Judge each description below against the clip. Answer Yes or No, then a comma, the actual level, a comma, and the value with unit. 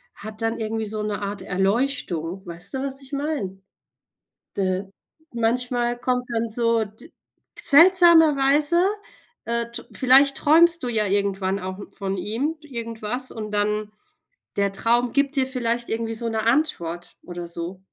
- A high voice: Yes, high, 230 Hz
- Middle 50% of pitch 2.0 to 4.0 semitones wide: No, average, 4.8 semitones